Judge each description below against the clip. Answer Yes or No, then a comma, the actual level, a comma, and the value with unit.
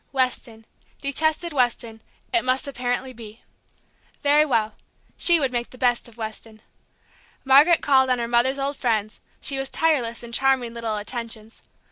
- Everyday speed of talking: Yes, average, 150 wpm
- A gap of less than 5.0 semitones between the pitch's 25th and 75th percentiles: Yes, average, 2.9 semitones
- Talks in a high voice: Yes, high, 245 Hz